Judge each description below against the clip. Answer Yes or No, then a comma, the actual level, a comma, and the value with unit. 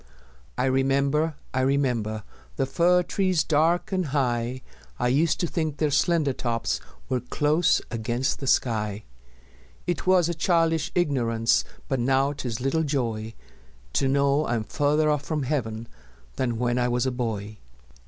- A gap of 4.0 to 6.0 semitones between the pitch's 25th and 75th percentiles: Yes, average, 4.3 semitones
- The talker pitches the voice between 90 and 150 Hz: Yes, low, 135 Hz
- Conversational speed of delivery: Yes, average, 150 wpm